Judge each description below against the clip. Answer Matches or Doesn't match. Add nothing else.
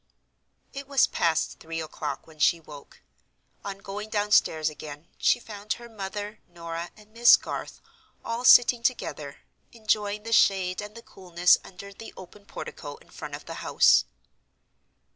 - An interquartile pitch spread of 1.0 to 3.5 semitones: Doesn't match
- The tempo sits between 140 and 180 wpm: Matches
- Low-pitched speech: Doesn't match